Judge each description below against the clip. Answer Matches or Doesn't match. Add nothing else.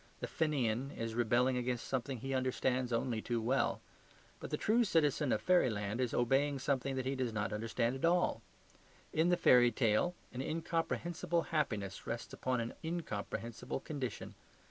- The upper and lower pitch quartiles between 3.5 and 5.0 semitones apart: Matches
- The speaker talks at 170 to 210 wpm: Doesn't match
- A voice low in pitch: Matches